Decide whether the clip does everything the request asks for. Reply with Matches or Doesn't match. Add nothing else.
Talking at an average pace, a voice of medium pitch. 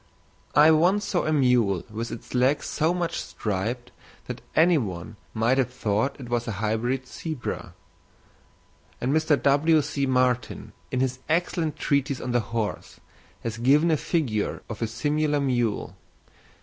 Doesn't match